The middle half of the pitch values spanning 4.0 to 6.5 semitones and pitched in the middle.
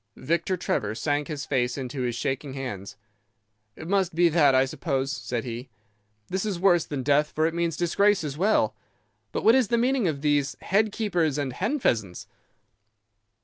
Yes: wide, 5.6 semitones; medium, 150 Hz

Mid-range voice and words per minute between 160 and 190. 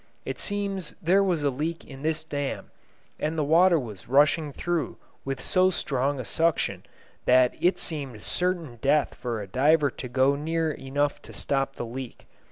Yes: medium, 145 Hz; average, 175 wpm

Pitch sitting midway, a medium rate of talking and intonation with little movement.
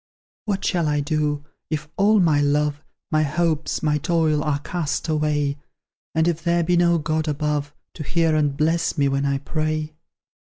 Yes: medium, 155 Hz; average, 170 wpm; narrow, 2.0 semitones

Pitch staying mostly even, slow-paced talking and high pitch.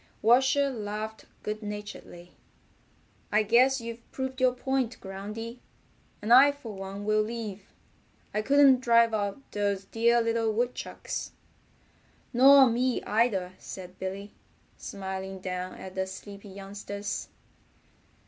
No: average, 3.5 semitones; slow, 120 wpm; high, 215 Hz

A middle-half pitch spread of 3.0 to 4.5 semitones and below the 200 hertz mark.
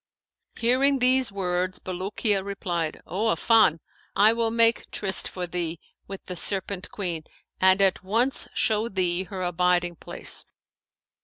Yes: average, 3.8 semitones; high, 190 Hz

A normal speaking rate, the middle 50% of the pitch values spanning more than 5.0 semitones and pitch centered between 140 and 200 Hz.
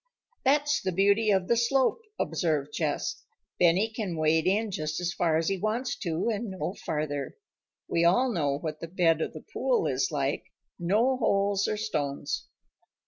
Yes: average, 170 wpm; wide, 5.5 semitones; high, 190 Hz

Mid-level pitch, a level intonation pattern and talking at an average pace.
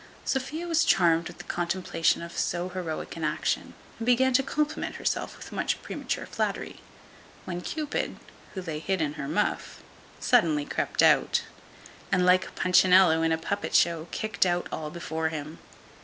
No: medium, 175 Hz; average, 3.2 semitones; average, 160 wpm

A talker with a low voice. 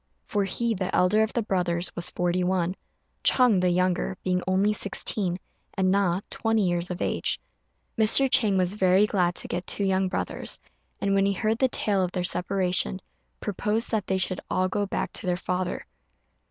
No: high, 190 Hz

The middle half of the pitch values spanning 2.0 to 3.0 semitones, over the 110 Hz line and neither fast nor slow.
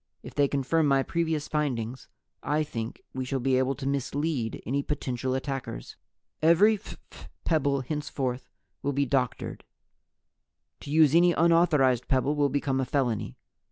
Yes: average, 2.7 semitones; medium, 140 Hz; average, 145 wpm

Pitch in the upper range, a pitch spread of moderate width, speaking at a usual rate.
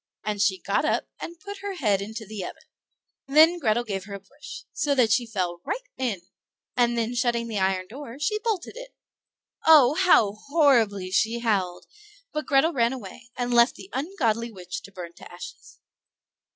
No: high, 235 Hz; wide, 6.5 semitones; average, 180 wpm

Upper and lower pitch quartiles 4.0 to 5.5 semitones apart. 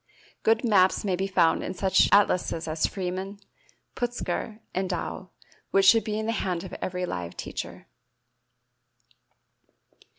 No: narrow, 2.6 semitones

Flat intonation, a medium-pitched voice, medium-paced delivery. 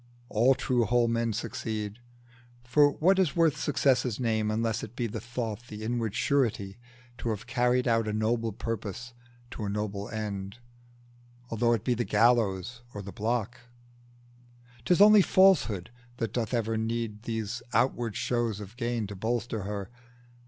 No: narrow, 2.3 semitones; low, 115 Hz; average, 155 wpm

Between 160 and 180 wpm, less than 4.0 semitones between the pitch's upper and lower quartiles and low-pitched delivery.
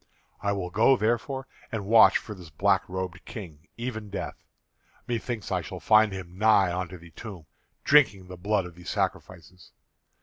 Yes: average, 170 wpm; average, 3.4 semitones; low, 100 Hz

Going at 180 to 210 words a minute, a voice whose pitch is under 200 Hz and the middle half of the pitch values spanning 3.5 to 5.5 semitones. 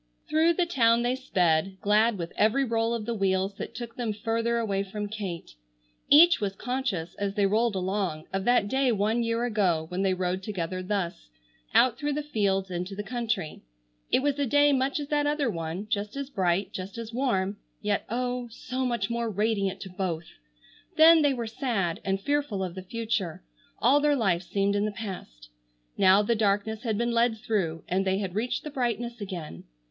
No: average, 195 wpm; high, 215 Hz; average, 4.0 semitones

